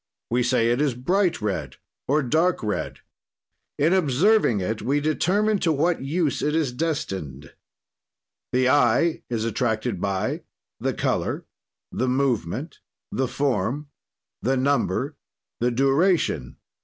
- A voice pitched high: No, low, 135 Hz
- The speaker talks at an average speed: No, slow, 125 wpm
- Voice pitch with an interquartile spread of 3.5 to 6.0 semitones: Yes, average, 4.9 semitones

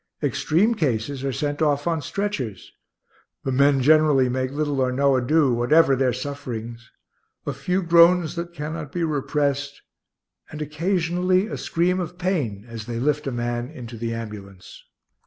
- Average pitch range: Yes, average, 5.0 semitones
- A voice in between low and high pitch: Yes, medium, 145 Hz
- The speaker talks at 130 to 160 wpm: Yes, average, 155 wpm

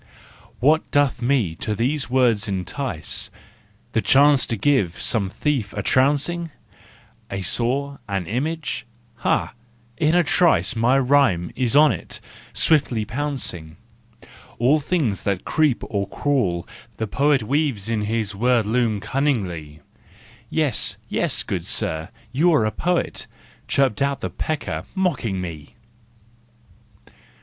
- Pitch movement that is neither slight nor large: No, wide, 6.1 semitones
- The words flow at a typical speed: No, slow, 125 wpm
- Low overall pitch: Yes, low, 125 Hz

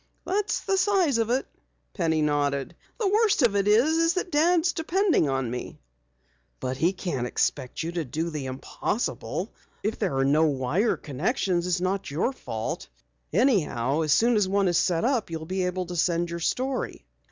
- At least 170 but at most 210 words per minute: Yes, average, 175 wpm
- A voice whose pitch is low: No, medium, 185 Hz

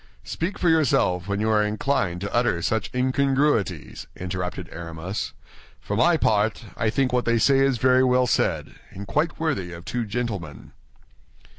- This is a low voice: Yes, low, 110 Hz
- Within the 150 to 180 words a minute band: Yes, average, 160 wpm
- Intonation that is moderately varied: No, wide, 5.9 semitones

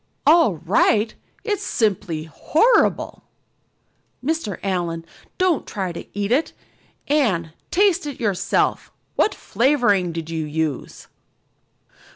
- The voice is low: No, high, 205 Hz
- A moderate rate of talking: No, slow, 105 wpm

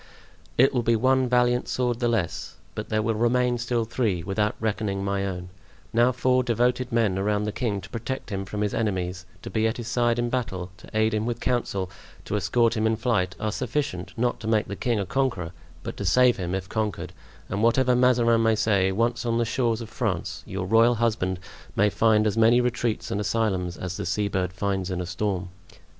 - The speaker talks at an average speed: No, fast, 210 wpm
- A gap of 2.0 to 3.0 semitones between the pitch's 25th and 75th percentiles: No, average, 3.6 semitones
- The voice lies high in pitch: No, low, 110 Hz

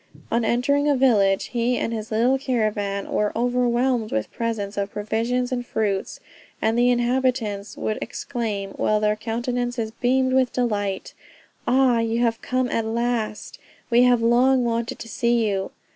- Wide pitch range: No, narrow, 2.4 semitones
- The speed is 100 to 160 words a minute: Yes, average, 155 wpm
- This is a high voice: Yes, high, 235 Hz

